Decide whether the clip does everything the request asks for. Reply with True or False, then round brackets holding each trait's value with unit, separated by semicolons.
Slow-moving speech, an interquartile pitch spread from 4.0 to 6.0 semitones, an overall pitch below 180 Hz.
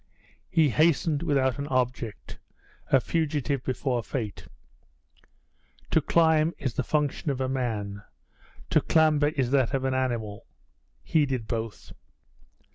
False (125 wpm; 3.6 semitones; 135 Hz)